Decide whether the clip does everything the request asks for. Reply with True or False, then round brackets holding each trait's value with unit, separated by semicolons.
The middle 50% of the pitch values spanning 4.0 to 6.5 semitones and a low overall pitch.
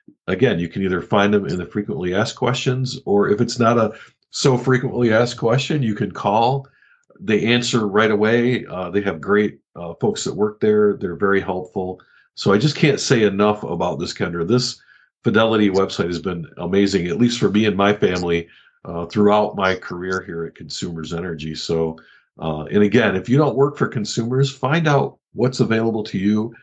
True (4.9 semitones; 110 Hz)